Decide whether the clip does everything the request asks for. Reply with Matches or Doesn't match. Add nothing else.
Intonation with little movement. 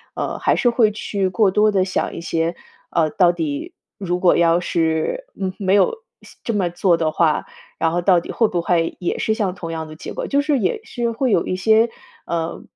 Doesn't match